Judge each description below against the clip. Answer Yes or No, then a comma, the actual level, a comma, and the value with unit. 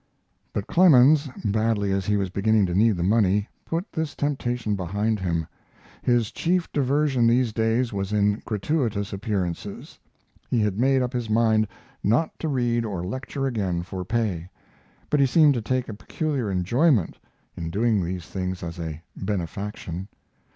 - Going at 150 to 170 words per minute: Yes, average, 160 wpm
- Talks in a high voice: No, low, 110 Hz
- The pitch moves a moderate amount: Yes, average, 4.5 semitones